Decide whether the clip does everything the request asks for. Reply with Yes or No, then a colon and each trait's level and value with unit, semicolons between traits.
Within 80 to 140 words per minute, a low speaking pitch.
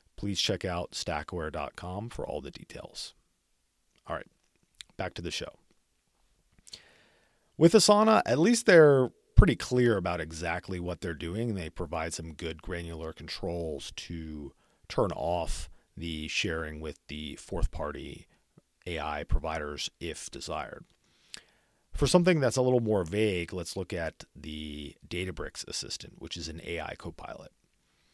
Yes: slow, 135 wpm; very low, 85 Hz